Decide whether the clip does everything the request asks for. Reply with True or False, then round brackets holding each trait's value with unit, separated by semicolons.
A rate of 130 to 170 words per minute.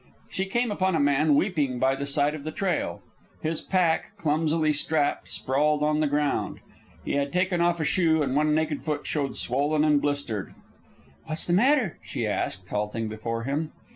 False (185 wpm)